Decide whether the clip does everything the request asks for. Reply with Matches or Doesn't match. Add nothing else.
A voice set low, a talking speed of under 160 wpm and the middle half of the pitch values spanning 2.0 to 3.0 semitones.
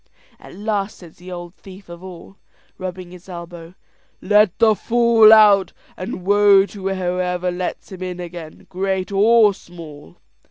Doesn't match